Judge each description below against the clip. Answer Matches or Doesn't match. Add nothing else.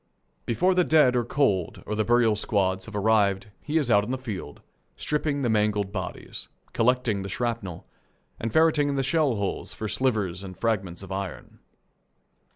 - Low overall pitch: Matches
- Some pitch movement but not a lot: Matches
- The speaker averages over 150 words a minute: Matches